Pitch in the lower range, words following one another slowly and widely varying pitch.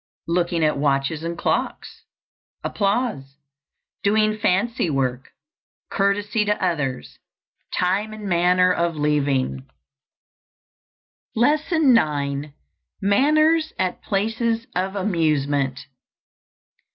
No: medium, 180 Hz; slow, 90 wpm; wide, 6.6 semitones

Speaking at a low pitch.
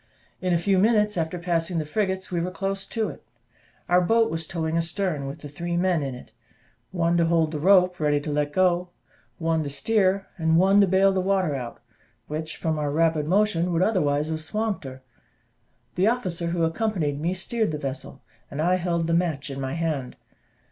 No: medium, 170 Hz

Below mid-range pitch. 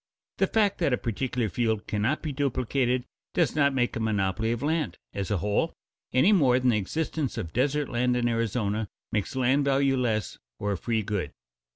Yes: low, 125 Hz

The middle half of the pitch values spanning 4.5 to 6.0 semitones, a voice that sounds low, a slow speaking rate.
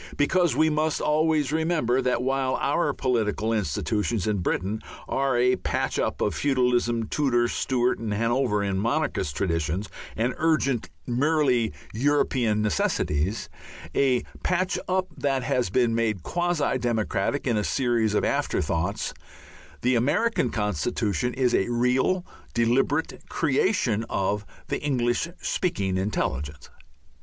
Yes: average, 5.0 semitones; low, 120 Hz; slow, 125 wpm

